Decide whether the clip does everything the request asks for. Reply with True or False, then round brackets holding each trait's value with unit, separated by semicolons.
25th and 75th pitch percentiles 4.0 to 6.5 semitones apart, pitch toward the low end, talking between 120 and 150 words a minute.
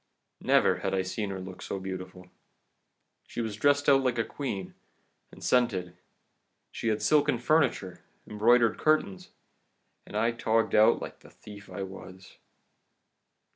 True (4.3 semitones; 110 Hz; 140 wpm)